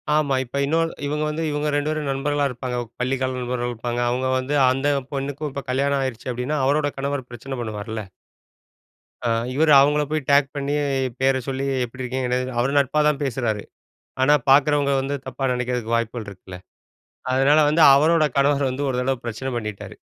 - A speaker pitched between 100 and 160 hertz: Yes, low, 135 Hz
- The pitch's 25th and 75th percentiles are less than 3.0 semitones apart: Yes, narrow, 2.5 semitones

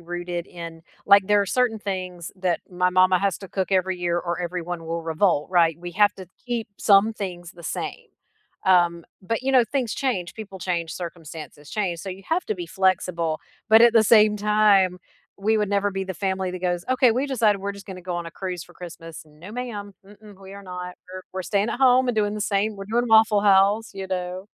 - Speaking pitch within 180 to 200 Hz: Yes, high, 190 Hz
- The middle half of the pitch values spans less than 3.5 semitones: Yes, average, 3.0 semitones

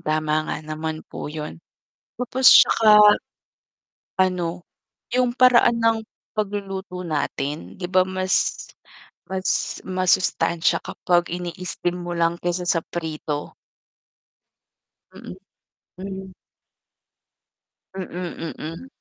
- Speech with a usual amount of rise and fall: Yes, average, 3.0 semitones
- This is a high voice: No, medium, 180 Hz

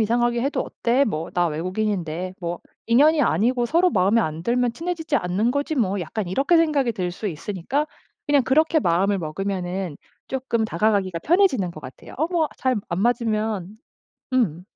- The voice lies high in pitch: Yes, high, 220 Hz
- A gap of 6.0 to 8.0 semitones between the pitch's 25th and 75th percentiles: Yes, wide, 6.7 semitones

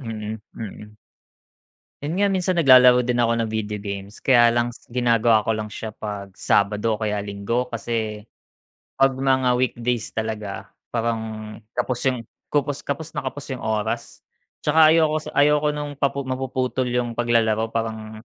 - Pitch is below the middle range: Yes, low, 120 Hz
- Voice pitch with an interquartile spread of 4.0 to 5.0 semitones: No, average, 3.3 semitones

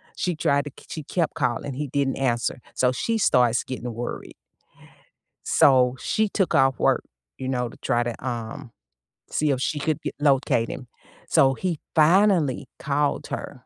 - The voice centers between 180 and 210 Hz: No, low, 135 Hz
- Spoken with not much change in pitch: No, average, 3.3 semitones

